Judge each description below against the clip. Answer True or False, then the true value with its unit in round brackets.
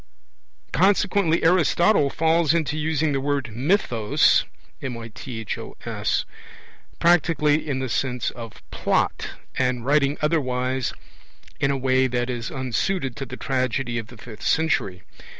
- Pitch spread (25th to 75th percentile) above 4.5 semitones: False (4.2 semitones)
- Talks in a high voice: False (135 Hz)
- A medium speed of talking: False (115 wpm)